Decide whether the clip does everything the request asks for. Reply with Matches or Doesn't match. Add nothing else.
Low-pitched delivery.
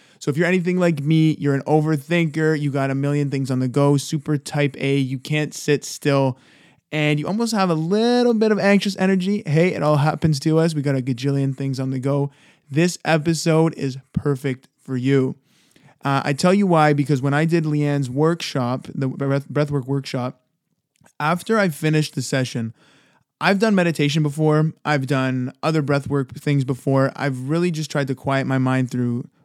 Doesn't match